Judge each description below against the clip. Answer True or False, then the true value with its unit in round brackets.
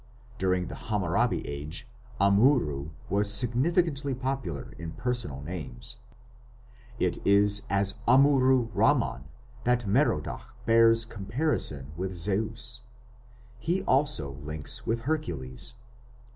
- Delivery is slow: True (100 wpm)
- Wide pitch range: True (7.7 semitones)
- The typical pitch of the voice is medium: False (105 Hz)